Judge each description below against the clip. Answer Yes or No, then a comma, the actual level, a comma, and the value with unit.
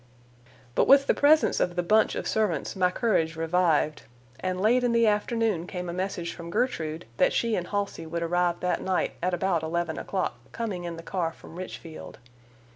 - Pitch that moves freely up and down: No, average, 3.9 semitones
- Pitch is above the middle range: No, medium, 180 Hz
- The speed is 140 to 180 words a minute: No, average, 190 wpm